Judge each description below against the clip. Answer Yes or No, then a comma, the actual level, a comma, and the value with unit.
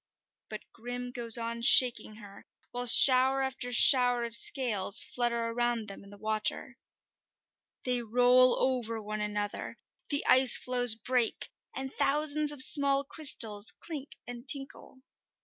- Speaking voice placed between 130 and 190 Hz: No, high, 245 Hz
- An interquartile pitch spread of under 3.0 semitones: Yes, narrow, 2.6 semitones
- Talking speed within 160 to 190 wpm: No, slow, 135 wpm